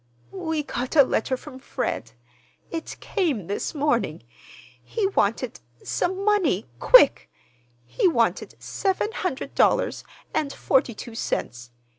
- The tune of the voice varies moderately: No, wide, 7.9 semitones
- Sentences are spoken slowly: Yes, slow, 115 wpm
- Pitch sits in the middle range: No, very high, 285 Hz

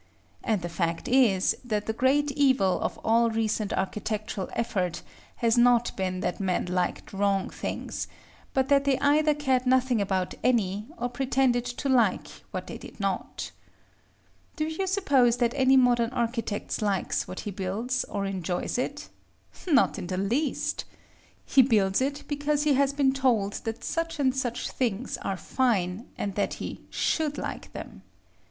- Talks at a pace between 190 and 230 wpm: No, average, 160 wpm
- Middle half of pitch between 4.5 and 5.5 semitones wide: Yes, average, 5.1 semitones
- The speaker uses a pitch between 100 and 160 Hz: No, high, 240 Hz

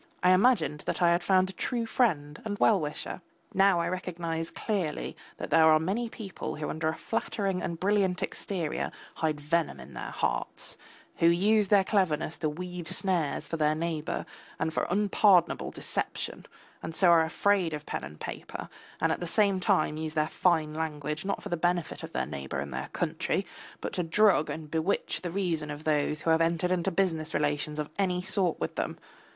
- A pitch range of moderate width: Yes, average, 3.5 semitones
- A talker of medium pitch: Yes, medium, 170 Hz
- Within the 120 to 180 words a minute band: No, average, 190 wpm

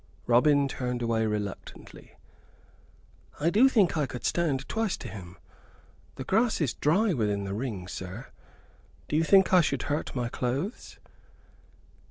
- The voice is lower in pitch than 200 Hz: Yes, low, 135 Hz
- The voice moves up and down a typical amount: No, wide, 7.4 semitones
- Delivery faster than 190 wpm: No, average, 145 wpm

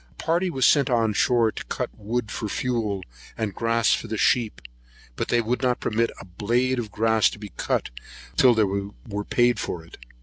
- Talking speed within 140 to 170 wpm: No, average, 200 wpm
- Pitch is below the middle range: Yes, low, 115 Hz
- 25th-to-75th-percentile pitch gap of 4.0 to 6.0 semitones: No, average, 2.8 semitones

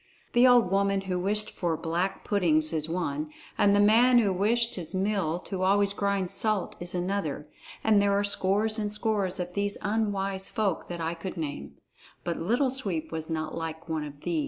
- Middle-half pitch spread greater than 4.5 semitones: No, average, 3.7 semitones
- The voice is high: Yes, high, 195 Hz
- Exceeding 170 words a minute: Yes, average, 190 wpm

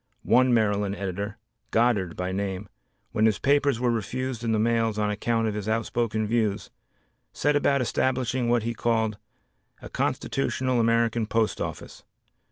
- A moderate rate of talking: Yes, average, 150 wpm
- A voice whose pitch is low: Yes, low, 115 Hz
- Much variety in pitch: No, narrow, 2.4 semitones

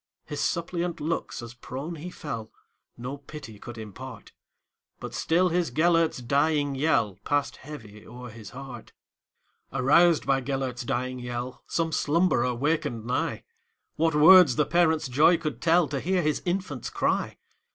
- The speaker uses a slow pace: Yes, slow, 120 wpm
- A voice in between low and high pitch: Yes, medium, 145 Hz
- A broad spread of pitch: No, average, 5.0 semitones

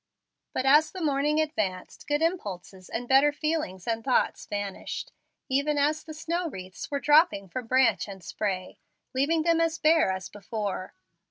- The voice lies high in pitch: Yes, very high, 270 Hz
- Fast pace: No, average, 160 wpm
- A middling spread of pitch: No, wide, 7.7 semitones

